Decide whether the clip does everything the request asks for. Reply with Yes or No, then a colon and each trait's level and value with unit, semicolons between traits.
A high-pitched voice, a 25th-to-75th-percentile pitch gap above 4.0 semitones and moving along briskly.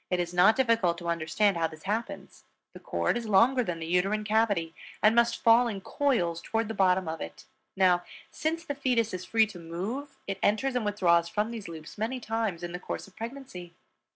Yes: high, 205 Hz; average, 4.8 semitones; fast, 210 wpm